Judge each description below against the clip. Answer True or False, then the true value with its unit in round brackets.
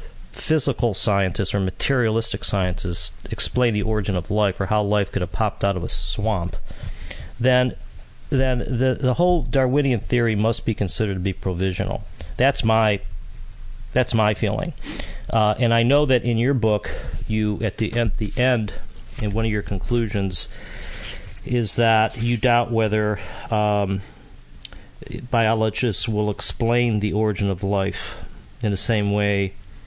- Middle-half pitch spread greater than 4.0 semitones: False (3.2 semitones)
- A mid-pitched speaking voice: False (105 Hz)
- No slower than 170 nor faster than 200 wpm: False (150 wpm)